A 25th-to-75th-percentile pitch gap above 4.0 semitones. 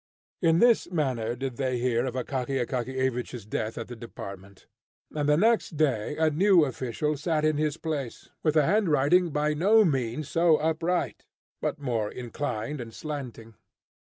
Yes: average, 4.4 semitones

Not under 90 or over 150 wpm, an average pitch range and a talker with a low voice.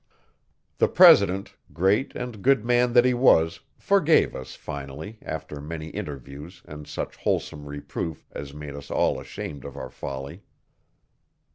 No: average, 140 wpm; wide, 7.7 semitones; very low, 80 Hz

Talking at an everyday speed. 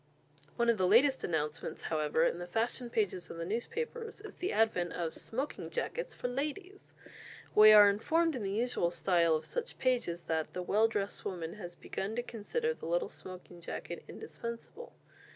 Yes: average, 175 wpm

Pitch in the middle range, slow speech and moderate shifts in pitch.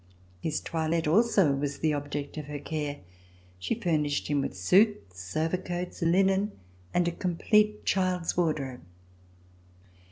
Yes: medium, 160 Hz; slow, 125 wpm; average, 4.1 semitones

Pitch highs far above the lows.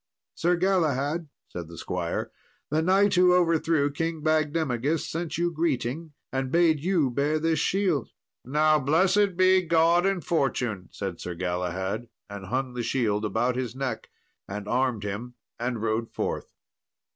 Yes: wide, 6.3 semitones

